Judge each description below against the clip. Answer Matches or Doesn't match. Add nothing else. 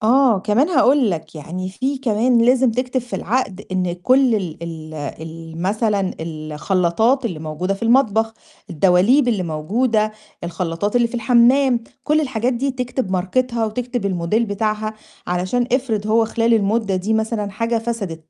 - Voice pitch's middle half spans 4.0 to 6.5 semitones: Matches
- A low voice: Doesn't match